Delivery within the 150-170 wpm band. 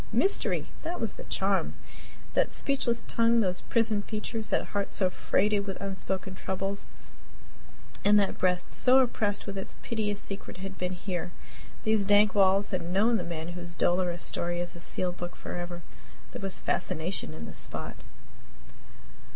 Yes: average, 160 wpm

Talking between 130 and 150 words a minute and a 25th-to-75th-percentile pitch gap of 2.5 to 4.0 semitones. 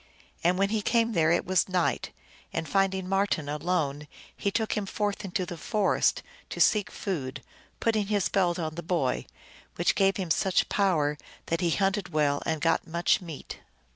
No: average, 175 wpm; average, 3.5 semitones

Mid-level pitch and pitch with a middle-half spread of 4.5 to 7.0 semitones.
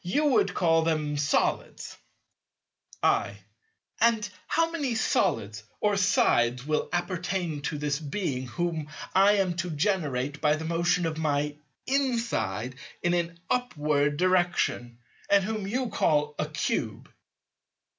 Yes: medium, 170 Hz; average, 5.2 semitones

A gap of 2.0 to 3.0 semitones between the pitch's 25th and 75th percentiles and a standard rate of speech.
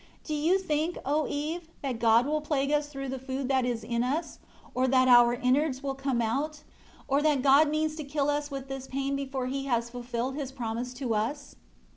No: average, 2.7 semitones; fast, 210 wpm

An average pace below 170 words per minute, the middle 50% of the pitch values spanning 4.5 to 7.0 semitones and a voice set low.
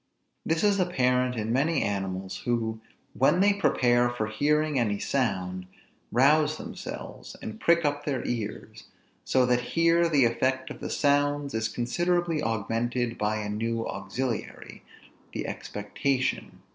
Yes: slow, 135 wpm; average, 4.8 semitones; low, 125 Hz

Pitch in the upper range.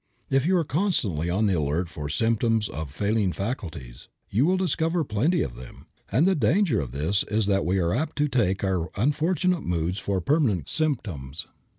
No: low, 105 Hz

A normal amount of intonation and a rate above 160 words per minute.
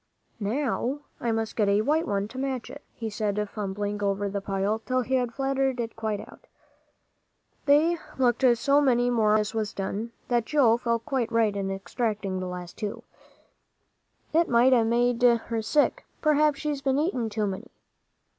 Yes: average, 4.1 semitones; average, 175 wpm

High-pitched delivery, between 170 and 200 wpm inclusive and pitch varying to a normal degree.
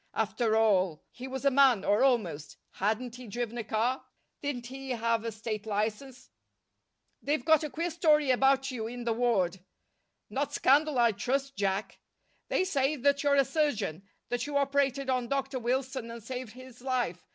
Yes: very high, 250 Hz; average, 175 wpm; average, 3.6 semitones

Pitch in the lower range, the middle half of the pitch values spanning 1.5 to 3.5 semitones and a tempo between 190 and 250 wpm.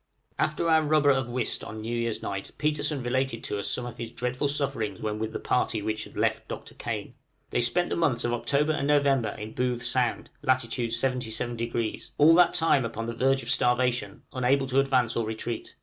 Yes: low, 125 Hz; average, 3.1 semitones; average, 200 wpm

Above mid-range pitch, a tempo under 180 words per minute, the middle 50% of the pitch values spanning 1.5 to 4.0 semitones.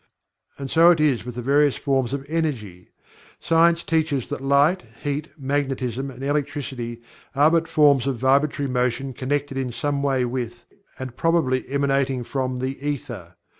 No: low, 135 Hz; average, 155 wpm; narrow, 2.4 semitones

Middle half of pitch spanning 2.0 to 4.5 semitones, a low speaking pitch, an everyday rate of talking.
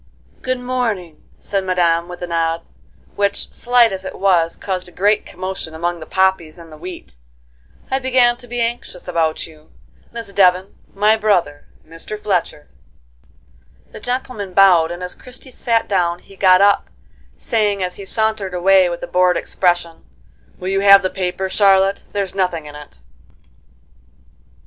No: average, 2.8 semitones; high, 190 Hz; average, 160 wpm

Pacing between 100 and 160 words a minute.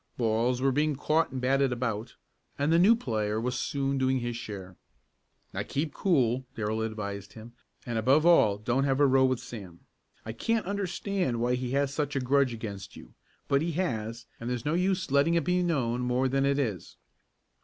No: average, 195 wpm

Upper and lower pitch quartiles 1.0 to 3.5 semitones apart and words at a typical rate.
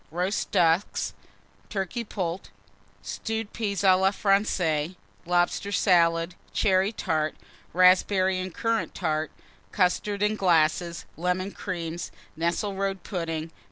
No: average, 2.9 semitones; slow, 105 wpm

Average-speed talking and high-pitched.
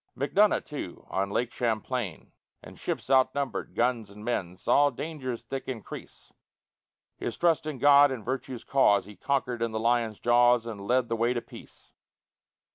No: average, 160 wpm; low, 120 Hz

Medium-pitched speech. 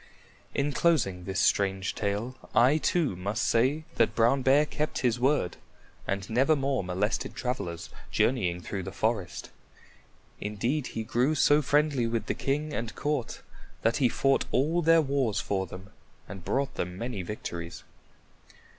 No: low, 120 Hz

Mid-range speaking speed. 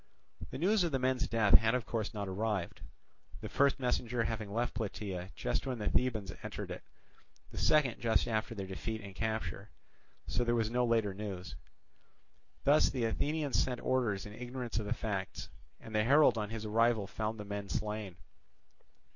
Yes: average, 180 wpm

